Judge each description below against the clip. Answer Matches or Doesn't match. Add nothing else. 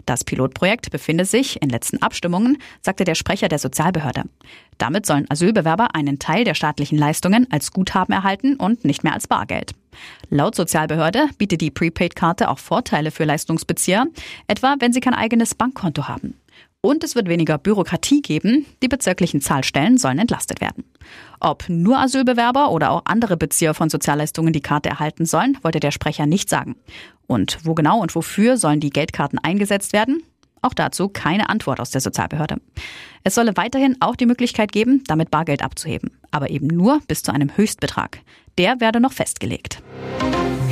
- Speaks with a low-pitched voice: Doesn't match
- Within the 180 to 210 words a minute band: Doesn't match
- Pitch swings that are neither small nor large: Doesn't match